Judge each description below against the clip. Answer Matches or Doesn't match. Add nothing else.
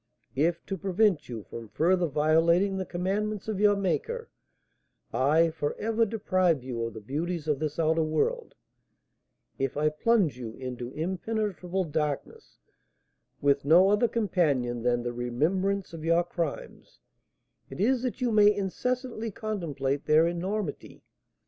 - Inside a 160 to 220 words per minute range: Doesn't match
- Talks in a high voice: Doesn't match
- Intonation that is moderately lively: Doesn't match